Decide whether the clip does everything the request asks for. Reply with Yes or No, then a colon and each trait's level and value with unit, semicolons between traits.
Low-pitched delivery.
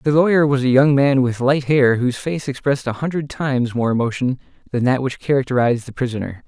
Yes: low, 130 Hz